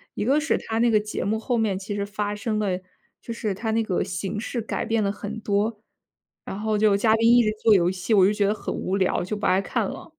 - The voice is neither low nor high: No, high, 210 Hz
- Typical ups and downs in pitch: No, narrow, 1.8 semitones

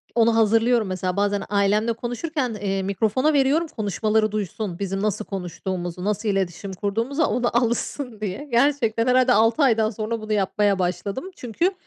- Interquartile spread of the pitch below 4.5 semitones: Yes, average, 3.3 semitones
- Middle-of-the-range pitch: No, high, 215 Hz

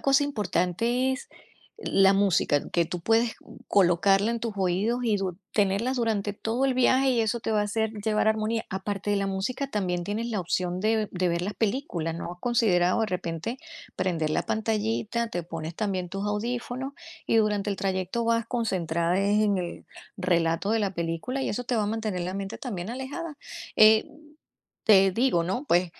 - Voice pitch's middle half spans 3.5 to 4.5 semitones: Yes, average, 4.1 semitones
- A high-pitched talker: Yes, high, 205 Hz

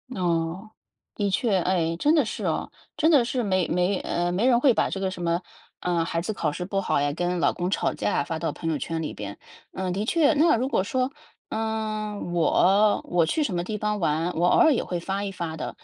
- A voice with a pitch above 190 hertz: No, medium, 185 Hz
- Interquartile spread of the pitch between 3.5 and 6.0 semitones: Yes, average, 4.2 semitones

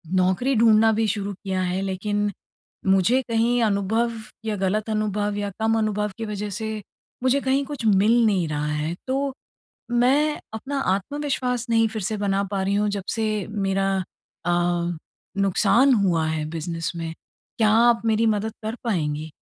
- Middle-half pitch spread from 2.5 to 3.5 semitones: Yes, average, 3.1 semitones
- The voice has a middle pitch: No, high, 210 Hz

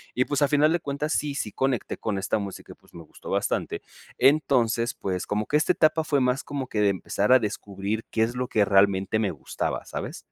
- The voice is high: No, low, 115 Hz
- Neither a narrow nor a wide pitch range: No, wide, 5.8 semitones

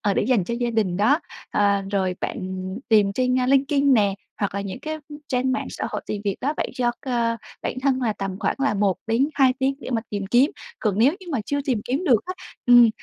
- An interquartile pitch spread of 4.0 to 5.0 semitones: Yes, average, 4.7 semitones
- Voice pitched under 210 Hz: No, high, 240 Hz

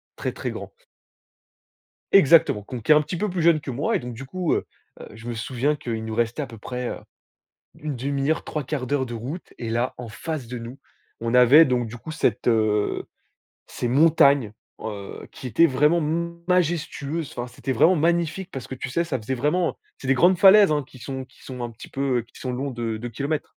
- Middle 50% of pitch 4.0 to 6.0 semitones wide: Yes, average, 4.7 semitones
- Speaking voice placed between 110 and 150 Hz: Yes, low, 135 Hz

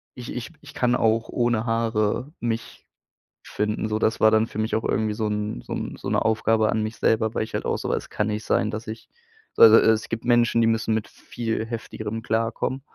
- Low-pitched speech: Yes, low, 110 Hz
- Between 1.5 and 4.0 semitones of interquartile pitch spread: No, narrow, 1.1 semitones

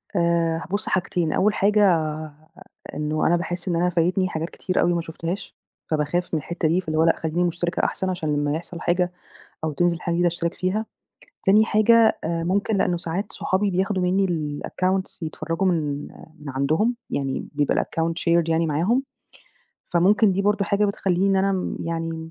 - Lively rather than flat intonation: No, average, 2.8 semitones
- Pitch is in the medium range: Yes, medium, 175 Hz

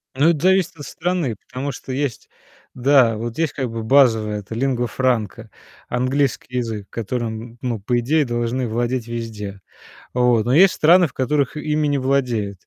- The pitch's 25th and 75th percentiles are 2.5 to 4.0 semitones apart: Yes, average, 3.7 semitones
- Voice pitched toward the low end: Yes, low, 125 Hz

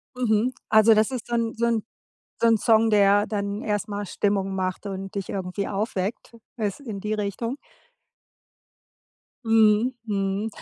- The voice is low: No, high, 210 Hz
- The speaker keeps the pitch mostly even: Yes, narrow, 2.1 semitones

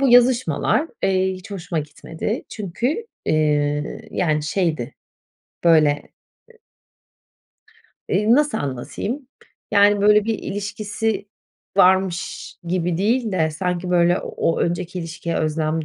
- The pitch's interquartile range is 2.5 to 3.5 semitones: No, average, 4.5 semitones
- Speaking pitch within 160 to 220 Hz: Yes, medium, 185 Hz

